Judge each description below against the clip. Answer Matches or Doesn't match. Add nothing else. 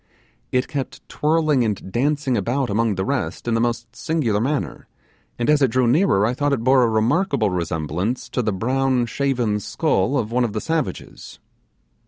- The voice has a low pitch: Matches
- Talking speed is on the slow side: Doesn't match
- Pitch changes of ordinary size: Matches